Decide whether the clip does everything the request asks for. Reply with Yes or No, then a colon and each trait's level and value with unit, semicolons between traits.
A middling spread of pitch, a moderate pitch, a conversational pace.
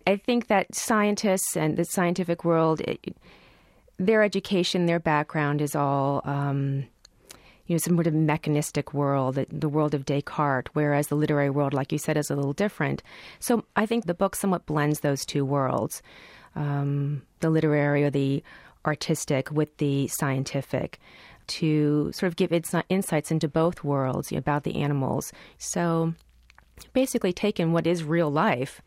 Yes: average, 3.4 semitones; medium, 155 Hz; average, 165 wpm